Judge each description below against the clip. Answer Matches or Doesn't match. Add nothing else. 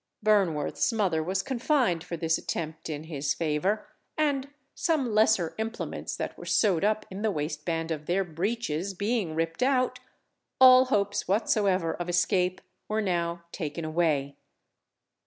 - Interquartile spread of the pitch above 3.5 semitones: Matches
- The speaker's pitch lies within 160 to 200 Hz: Matches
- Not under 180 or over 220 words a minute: Doesn't match